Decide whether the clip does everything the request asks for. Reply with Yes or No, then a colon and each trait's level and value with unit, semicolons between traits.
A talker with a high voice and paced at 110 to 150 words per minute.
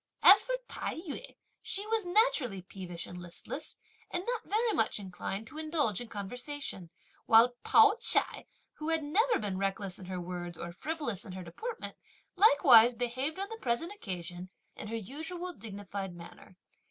No: high, 235 Hz; average, 165 wpm